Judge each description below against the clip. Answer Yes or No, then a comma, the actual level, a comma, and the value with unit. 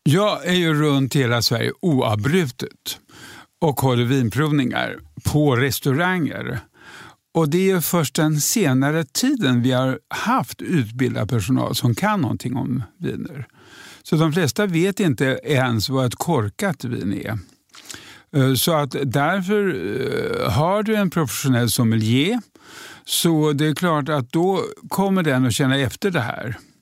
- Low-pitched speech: No, medium, 145 Hz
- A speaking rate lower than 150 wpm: Yes, average, 140 wpm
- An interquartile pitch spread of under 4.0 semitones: No, wide, 5.6 semitones